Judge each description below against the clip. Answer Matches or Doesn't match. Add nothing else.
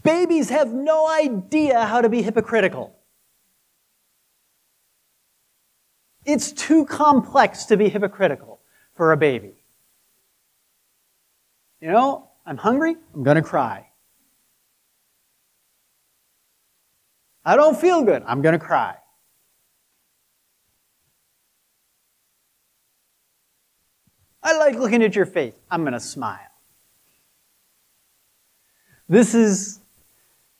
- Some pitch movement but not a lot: Doesn't match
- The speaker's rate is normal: Doesn't match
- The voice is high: Matches